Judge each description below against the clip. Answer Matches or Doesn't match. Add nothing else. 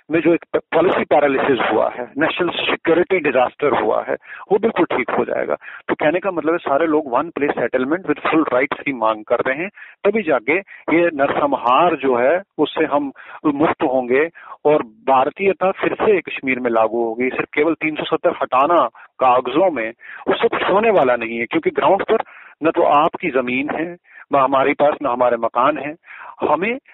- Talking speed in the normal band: Matches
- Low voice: Doesn't match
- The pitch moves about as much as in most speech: Matches